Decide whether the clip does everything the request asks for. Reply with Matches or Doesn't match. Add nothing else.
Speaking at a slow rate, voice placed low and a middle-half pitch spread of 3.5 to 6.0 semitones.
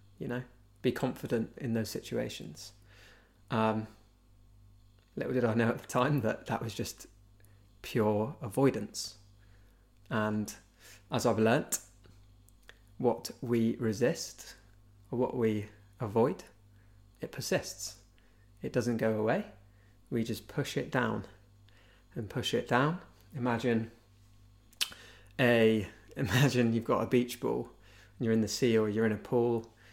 Doesn't match